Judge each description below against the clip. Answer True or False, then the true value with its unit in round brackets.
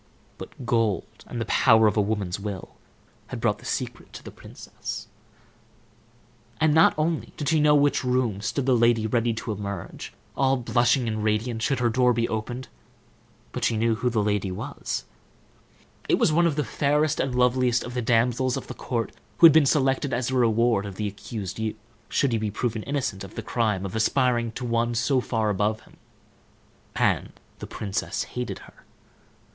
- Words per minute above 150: True (190 wpm)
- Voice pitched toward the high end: False (120 Hz)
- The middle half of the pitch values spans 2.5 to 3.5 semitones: True (3.1 semitones)